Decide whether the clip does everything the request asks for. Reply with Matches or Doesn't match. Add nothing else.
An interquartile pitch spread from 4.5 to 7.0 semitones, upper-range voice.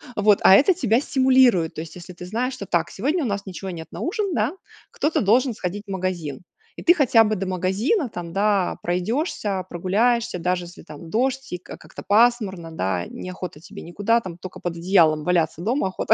Matches